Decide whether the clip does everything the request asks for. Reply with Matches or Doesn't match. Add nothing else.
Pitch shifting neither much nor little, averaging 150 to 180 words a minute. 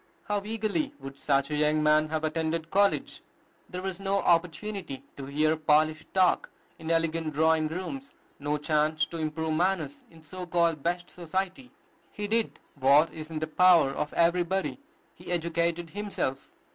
Matches